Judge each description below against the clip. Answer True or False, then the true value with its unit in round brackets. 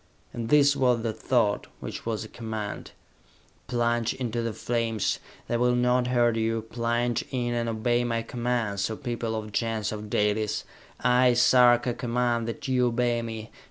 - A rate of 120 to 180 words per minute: True (165 wpm)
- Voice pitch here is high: False (120 Hz)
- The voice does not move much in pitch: True (1.6 semitones)